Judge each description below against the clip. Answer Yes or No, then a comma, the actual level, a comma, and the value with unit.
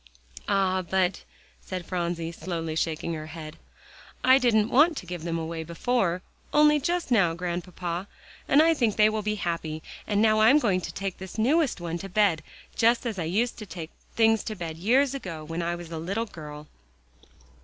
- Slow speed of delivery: No, average, 185 wpm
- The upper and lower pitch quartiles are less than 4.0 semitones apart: No, average, 5.0 semitones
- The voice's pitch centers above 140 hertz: Yes, medium, 185 Hz